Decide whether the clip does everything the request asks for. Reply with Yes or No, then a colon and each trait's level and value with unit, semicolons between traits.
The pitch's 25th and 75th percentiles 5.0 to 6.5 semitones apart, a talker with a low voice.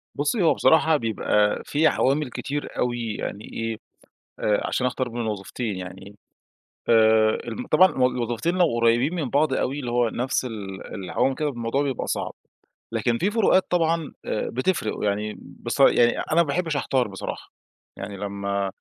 Yes: average, 5.3 semitones; low, 120 Hz